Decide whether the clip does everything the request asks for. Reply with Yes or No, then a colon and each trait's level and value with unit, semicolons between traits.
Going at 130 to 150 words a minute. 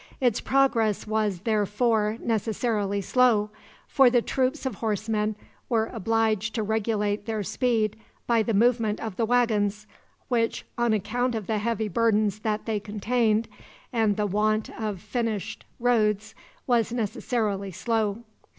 Yes: slow, 135 wpm